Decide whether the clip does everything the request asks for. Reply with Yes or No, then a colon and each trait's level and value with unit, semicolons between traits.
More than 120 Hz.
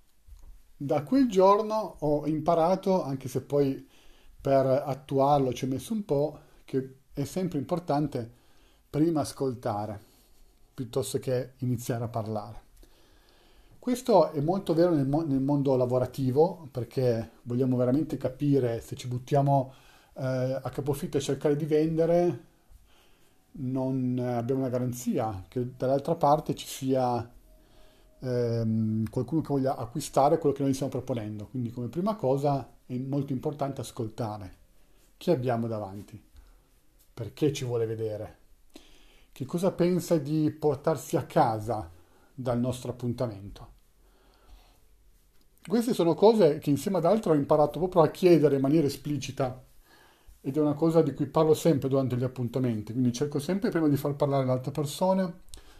Yes: low, 135 Hz